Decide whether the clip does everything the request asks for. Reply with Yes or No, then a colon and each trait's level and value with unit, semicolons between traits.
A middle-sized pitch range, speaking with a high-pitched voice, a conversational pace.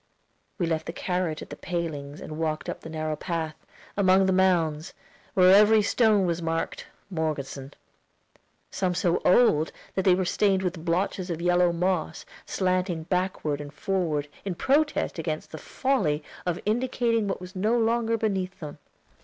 No: average, 3.3 semitones; medium, 180 Hz; average, 160 wpm